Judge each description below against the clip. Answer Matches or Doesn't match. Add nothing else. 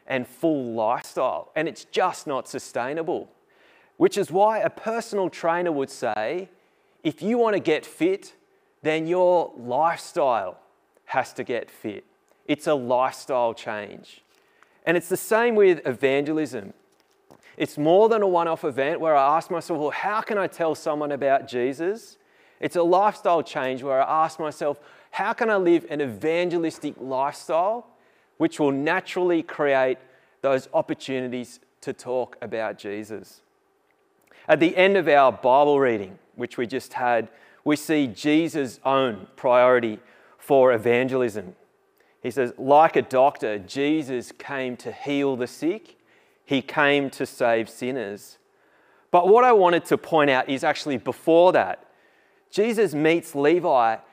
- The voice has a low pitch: Doesn't match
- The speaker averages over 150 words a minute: Doesn't match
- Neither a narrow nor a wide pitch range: Doesn't match